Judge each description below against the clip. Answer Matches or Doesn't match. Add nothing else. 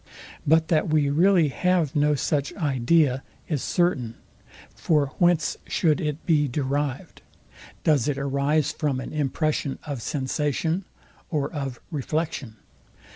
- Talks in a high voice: Doesn't match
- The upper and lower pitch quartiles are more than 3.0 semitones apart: Doesn't match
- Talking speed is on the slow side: Matches